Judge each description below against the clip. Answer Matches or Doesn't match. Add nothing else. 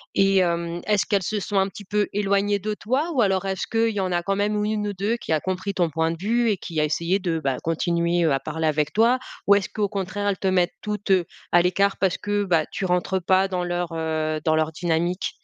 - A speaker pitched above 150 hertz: Matches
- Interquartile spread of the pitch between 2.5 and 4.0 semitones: Matches